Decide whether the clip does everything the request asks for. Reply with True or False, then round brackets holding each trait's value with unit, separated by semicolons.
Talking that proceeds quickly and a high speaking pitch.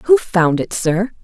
False (195 wpm; 210 Hz)